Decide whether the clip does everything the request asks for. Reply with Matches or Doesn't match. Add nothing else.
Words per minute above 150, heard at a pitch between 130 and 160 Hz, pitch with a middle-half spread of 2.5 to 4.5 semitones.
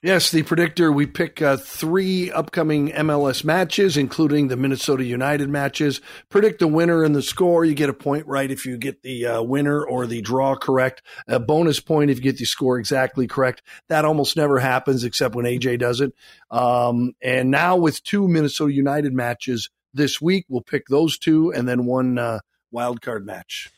Matches